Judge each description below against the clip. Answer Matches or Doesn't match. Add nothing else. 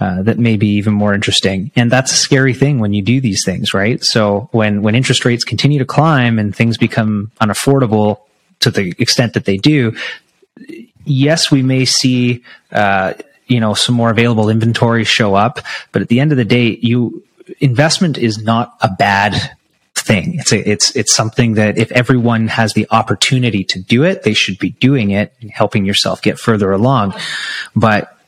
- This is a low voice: Matches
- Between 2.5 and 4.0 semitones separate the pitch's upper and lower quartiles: Matches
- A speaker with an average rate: Matches